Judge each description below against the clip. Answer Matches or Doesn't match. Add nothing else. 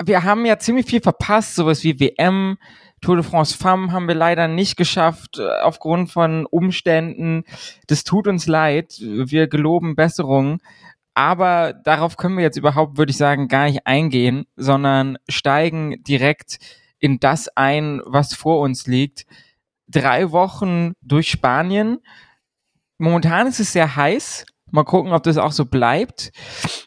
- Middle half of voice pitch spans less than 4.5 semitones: Matches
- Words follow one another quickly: Doesn't match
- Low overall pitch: Doesn't match